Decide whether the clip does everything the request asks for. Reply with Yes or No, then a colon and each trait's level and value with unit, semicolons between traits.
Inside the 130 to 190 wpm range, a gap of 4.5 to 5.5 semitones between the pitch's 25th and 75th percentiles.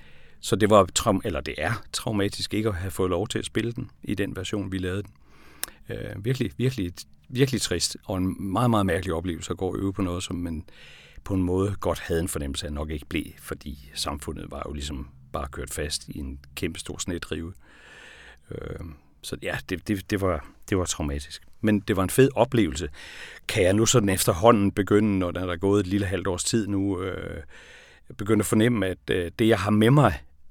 No: average, 210 wpm; average, 5.1 semitones